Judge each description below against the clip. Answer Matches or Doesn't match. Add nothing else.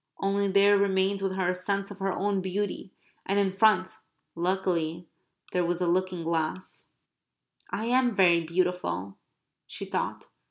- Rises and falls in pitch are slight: Matches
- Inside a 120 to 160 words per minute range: Matches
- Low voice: Doesn't match